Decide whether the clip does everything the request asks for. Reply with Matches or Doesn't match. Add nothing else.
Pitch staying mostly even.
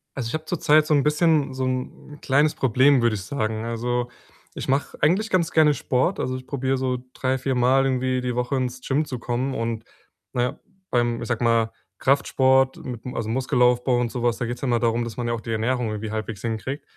Matches